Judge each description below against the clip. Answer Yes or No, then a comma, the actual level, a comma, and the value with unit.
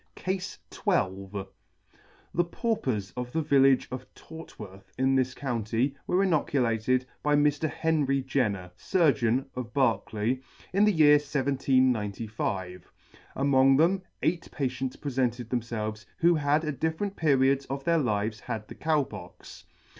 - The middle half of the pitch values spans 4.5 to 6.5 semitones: Yes, average, 4.8 semitones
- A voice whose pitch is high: No, low, 130 Hz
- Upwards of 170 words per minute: No, slow, 135 wpm